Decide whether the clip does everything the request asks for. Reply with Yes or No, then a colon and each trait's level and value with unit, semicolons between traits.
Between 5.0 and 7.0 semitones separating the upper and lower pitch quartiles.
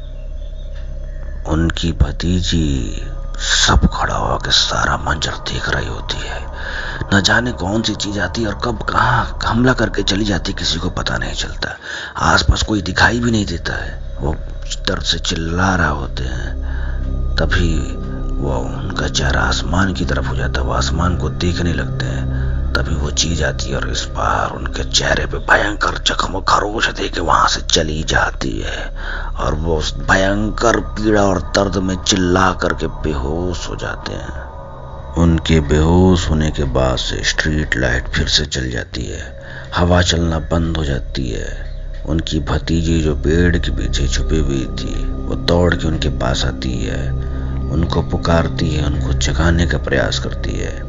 No: average, 4.6 semitones